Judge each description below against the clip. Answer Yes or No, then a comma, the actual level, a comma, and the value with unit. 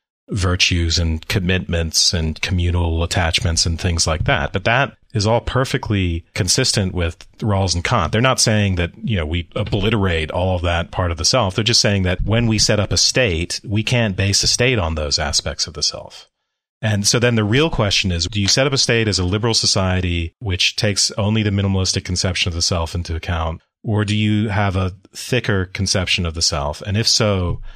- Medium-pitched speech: No, very low, 95 Hz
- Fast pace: Yes, fast, 210 wpm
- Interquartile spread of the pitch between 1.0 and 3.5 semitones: No, average, 3.9 semitones